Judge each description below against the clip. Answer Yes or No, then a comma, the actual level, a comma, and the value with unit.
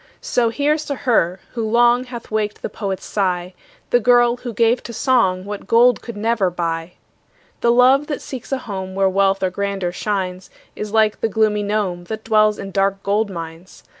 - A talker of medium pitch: No, high, 210 Hz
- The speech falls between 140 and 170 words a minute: No, average, 190 wpm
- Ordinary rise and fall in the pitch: Yes, average, 3.8 semitones